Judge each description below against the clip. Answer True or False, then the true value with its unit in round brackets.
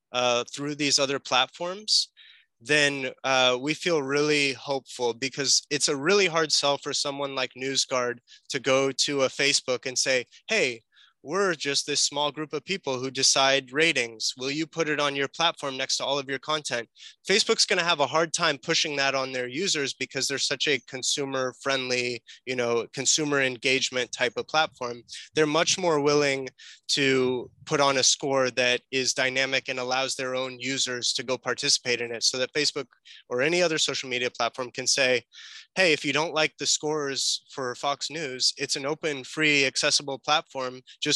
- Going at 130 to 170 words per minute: False (185 wpm)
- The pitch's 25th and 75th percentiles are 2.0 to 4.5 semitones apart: True (2.6 semitones)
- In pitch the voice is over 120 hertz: True (135 Hz)